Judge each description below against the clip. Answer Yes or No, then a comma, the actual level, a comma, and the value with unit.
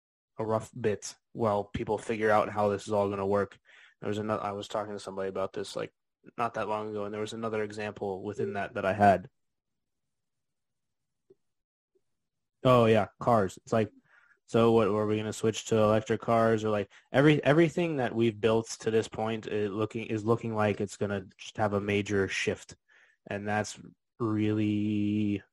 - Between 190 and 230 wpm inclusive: No, average, 180 wpm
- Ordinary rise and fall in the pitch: No, narrow, 1.6 semitones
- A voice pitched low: Yes, low, 105 Hz